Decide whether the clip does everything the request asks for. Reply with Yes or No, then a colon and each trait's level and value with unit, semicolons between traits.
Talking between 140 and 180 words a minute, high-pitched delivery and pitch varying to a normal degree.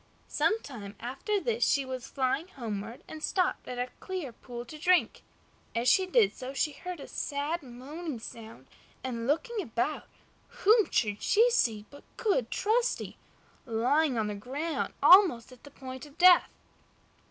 No: average, 160 wpm; very high, 280 Hz; wide, 7.0 semitones